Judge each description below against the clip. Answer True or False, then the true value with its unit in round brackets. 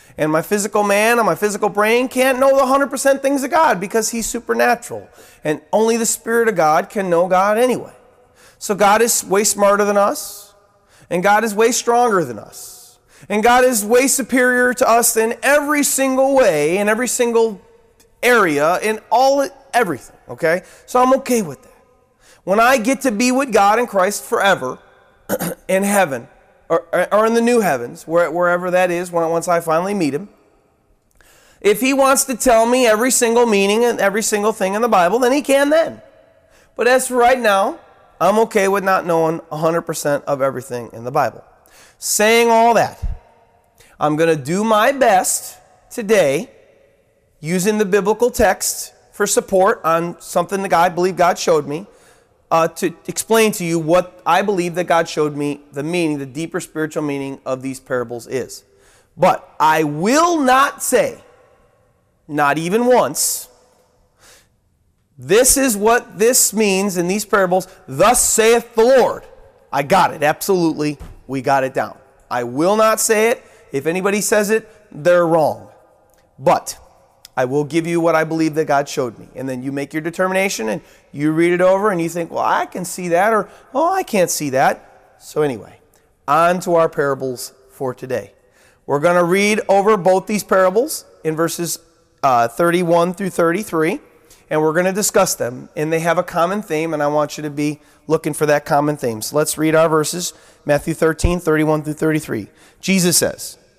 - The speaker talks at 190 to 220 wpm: False (175 wpm)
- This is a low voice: False (190 Hz)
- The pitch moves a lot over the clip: True (6.3 semitones)